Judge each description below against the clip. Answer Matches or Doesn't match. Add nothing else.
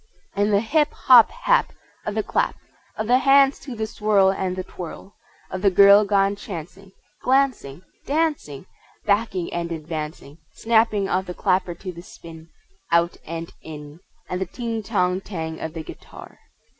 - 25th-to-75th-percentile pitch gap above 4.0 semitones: Matches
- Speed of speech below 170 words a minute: Matches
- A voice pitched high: Matches